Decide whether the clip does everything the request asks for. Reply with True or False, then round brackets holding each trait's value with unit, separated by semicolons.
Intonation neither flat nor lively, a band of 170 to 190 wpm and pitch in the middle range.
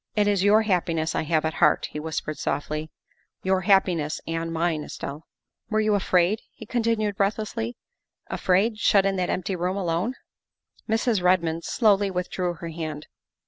True (3.8 semitones; 175 wpm; 180 Hz)